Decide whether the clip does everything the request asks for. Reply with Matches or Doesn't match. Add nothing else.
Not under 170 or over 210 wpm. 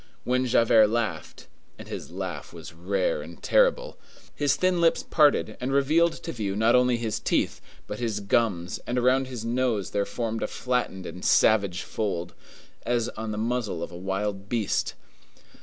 Doesn't match